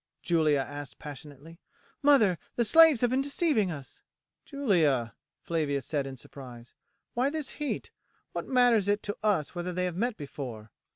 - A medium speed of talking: Yes, average, 155 wpm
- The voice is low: No, medium, 175 Hz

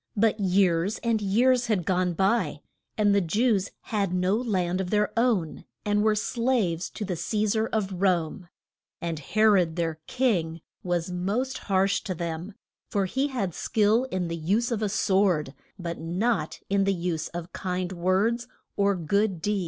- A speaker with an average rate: Yes, average, 175 wpm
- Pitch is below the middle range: No, high, 195 Hz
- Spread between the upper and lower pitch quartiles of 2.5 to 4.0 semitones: Yes, average, 3.5 semitones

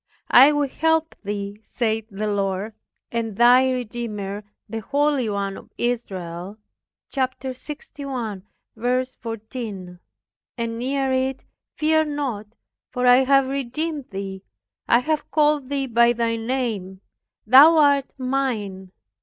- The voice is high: Yes, high, 245 Hz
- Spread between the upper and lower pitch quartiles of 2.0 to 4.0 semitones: No, average, 4.5 semitones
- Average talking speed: No, slow, 115 wpm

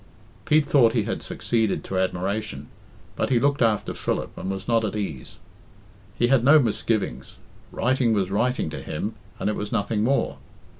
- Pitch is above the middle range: No, low, 110 Hz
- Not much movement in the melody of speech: No, average, 4.0 semitones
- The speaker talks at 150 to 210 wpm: Yes, average, 170 wpm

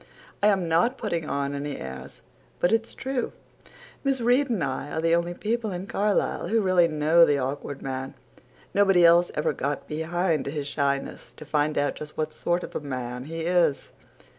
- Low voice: No, medium, 165 Hz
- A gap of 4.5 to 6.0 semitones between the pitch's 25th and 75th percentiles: Yes, average, 4.9 semitones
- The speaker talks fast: No, average, 185 wpm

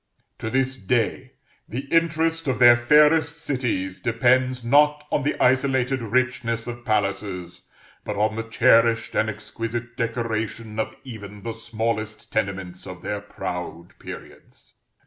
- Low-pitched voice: Yes, low, 115 Hz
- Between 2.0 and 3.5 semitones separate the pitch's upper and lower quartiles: Yes, average, 3.1 semitones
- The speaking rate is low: Yes, slow, 130 wpm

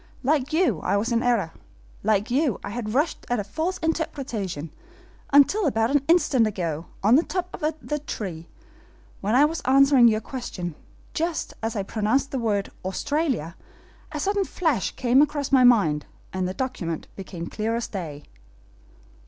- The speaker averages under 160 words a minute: No, average, 165 wpm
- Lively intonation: Yes, wide, 6.5 semitones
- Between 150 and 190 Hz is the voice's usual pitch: No, high, 240 Hz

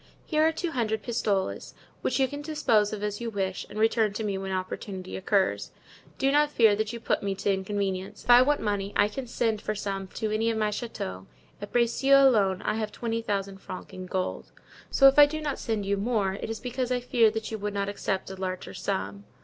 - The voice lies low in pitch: No, high, 210 Hz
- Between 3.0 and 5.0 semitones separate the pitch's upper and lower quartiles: Yes, average, 3.4 semitones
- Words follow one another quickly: Yes, fast, 225 wpm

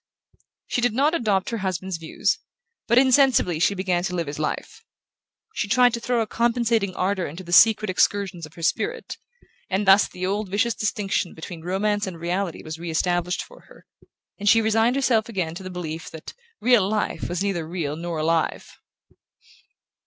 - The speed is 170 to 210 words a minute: Yes, average, 180 wpm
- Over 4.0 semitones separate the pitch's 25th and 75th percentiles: Yes, average, 4.4 semitones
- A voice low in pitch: No, high, 190 Hz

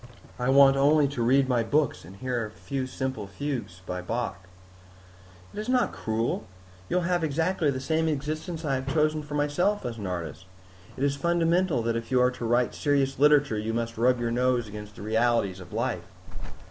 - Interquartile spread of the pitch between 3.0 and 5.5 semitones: Yes, average, 4.5 semitones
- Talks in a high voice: No, low, 130 Hz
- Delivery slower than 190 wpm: No, average, 200 wpm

